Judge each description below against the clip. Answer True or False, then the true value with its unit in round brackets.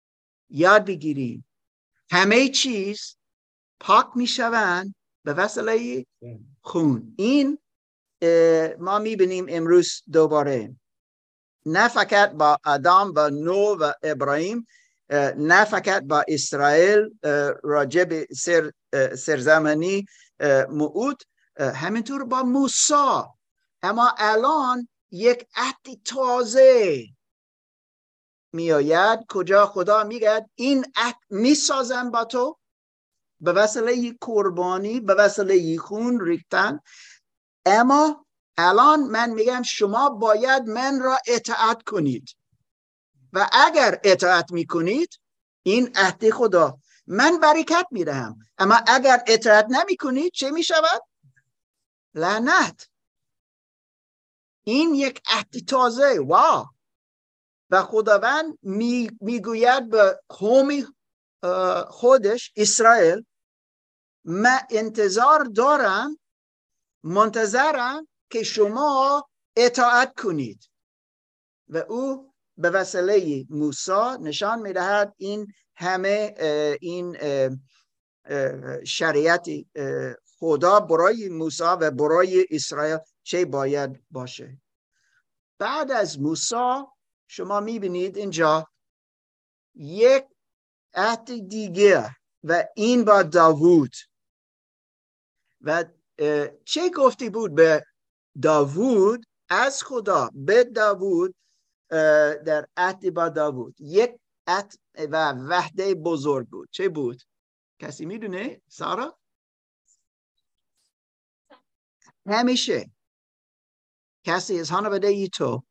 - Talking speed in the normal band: False (90 wpm)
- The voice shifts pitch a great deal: True (7.8 semitones)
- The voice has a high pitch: True (205 Hz)